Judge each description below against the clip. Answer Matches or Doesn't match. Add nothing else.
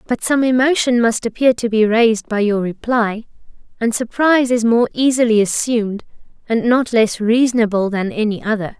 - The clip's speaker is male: Doesn't match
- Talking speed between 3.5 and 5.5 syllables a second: Matches